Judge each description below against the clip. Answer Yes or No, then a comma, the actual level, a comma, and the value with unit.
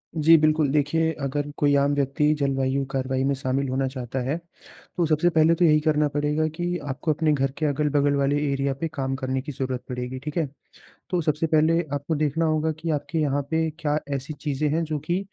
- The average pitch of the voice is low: No, medium, 145 Hz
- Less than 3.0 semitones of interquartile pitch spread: Yes, narrow, 2.5 semitones